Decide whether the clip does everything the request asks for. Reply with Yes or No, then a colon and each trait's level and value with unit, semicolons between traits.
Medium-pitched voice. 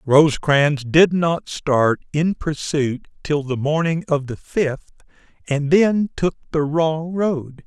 Yes: medium, 155 Hz